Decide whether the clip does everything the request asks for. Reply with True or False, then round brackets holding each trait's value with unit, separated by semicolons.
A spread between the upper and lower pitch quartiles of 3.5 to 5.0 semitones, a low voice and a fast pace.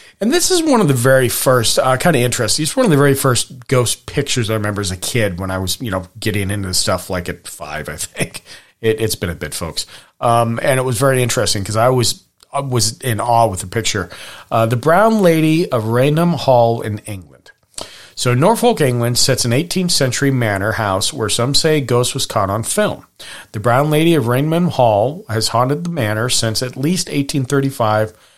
True (4.4 semitones; 125 Hz; 215 wpm)